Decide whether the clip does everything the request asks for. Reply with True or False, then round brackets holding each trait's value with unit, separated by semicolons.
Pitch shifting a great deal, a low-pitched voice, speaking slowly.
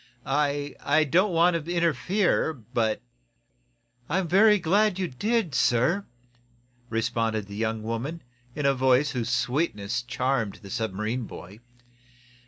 True (6.6 semitones; 130 Hz; 130 wpm)